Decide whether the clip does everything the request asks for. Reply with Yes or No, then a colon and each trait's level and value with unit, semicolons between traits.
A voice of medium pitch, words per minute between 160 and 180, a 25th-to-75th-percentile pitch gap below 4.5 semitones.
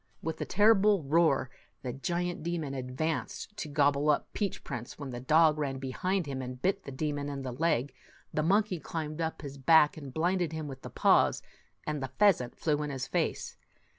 No: medium, 150 Hz; average, 195 wpm; average, 3.9 semitones